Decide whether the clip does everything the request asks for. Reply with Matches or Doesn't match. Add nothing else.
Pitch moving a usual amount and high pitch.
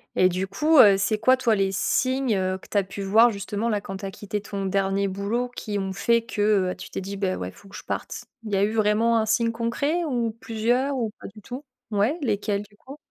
Matches